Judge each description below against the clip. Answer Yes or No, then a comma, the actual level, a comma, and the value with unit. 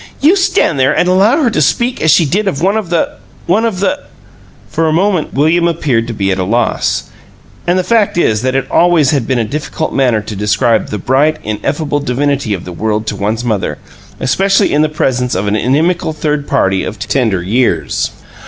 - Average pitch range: No, wide, 7.6 semitones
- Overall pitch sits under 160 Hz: Yes, medium, 140 Hz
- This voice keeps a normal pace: No, fast, 210 wpm